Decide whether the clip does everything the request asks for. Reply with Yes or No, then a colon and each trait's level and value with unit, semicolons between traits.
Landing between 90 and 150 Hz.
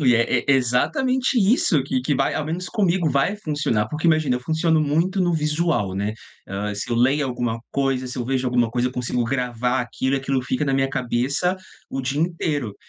Yes: low, 135 Hz